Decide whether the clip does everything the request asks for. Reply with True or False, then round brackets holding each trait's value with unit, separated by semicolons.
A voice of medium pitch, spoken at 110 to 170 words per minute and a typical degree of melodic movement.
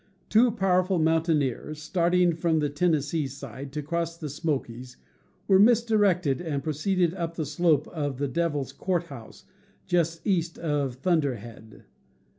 True (160 Hz; 140 wpm; 3.8 semitones)